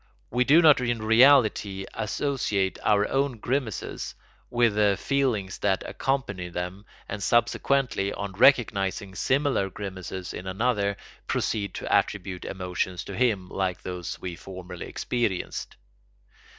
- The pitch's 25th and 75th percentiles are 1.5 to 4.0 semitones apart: No, average, 4.6 semitones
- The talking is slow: Yes, slow, 125 wpm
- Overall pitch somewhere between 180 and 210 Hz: No, low, 100 Hz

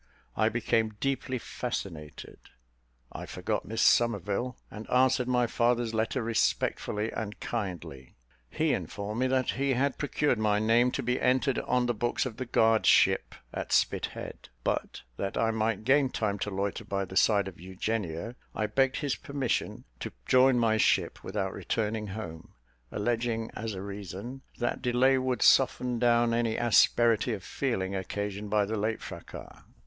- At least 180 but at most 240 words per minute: No, average, 160 wpm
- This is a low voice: Yes, low, 115 Hz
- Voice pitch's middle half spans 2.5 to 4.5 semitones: Yes, average, 3.3 semitones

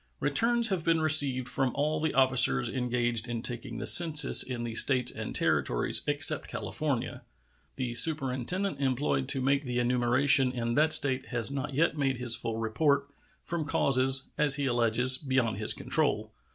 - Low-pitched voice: Yes, low, 130 Hz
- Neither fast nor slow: Yes, average, 165 wpm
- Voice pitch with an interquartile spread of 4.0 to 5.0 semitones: No, average, 3.1 semitones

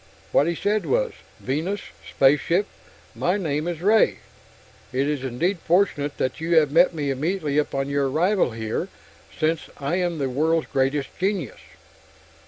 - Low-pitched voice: No, medium, 155 Hz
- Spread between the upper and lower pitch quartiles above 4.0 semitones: Yes, average, 4.4 semitones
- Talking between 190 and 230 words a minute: No, average, 150 wpm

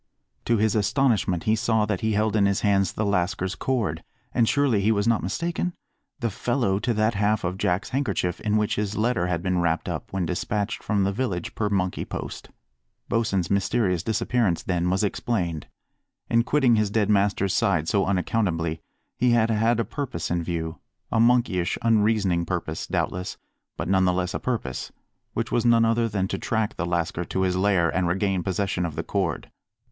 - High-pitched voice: No, low, 100 Hz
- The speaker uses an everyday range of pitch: Yes, average, 3.8 semitones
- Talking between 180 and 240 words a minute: Yes, average, 190 wpm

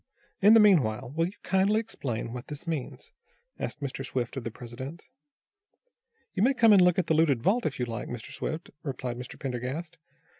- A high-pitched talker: No, medium, 145 Hz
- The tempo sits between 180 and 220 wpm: Yes, average, 190 wpm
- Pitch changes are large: Yes, wide, 6.8 semitones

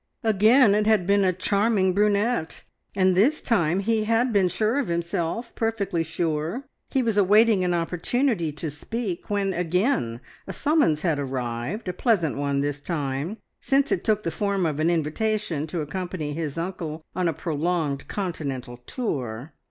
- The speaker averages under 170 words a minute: Yes, average, 160 wpm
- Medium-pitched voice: Yes, medium, 180 Hz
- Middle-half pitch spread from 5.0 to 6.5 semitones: Yes, wide, 5.5 semitones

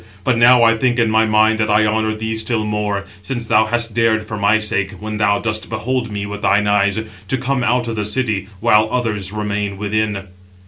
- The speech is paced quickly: Yes, fast, 215 wpm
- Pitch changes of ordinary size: No, narrow, 1.8 semitones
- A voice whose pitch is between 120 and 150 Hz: No, low, 110 Hz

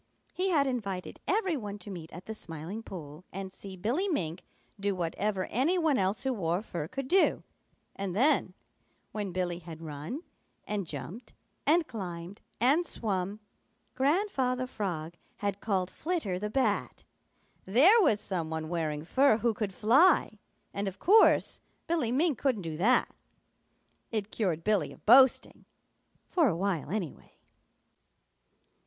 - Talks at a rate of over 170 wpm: No, average, 145 wpm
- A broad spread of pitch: Yes, wide, 6.7 semitones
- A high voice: Yes, high, 205 Hz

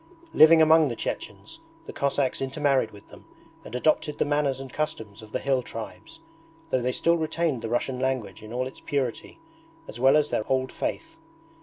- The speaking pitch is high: No, low, 135 Hz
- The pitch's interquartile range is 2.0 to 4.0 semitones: Yes, average, 3.6 semitones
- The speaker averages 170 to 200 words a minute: Yes, average, 185 wpm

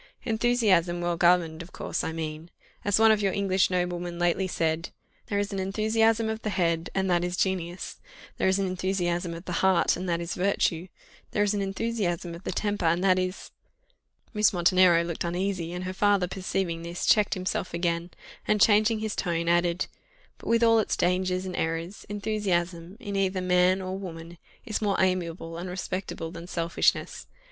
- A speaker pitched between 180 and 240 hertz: Yes, medium, 185 Hz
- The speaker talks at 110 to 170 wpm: No, average, 185 wpm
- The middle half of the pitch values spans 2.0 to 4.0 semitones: Yes, narrow, 2.6 semitones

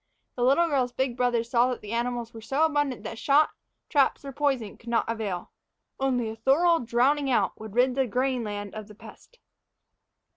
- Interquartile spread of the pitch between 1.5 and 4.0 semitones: Yes, average, 3.1 semitones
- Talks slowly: No, average, 190 wpm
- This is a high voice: Yes, high, 245 Hz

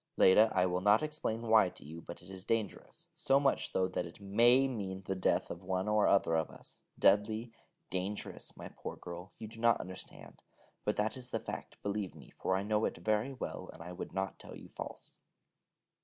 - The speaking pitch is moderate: No, low, 100 Hz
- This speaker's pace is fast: Yes, fast, 215 wpm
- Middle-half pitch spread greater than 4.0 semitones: No, average, 3.3 semitones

